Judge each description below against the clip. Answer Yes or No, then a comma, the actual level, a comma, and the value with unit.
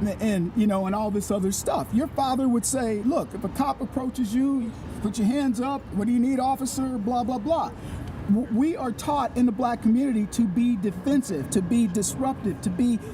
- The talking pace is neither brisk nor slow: No, fast, 210 wpm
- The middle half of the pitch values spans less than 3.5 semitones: No, average, 3.8 semitones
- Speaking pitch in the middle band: No, high, 240 Hz